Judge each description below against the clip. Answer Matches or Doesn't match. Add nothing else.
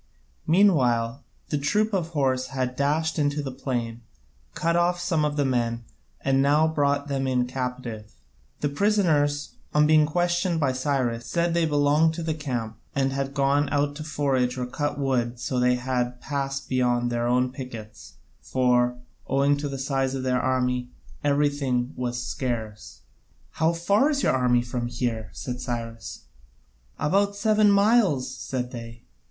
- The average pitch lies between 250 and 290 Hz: Doesn't match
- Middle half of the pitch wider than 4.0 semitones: Doesn't match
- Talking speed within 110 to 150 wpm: Doesn't match